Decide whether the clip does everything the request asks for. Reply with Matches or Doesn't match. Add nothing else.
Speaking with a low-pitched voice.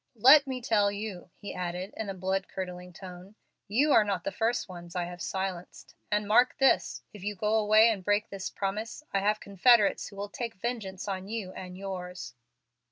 Doesn't match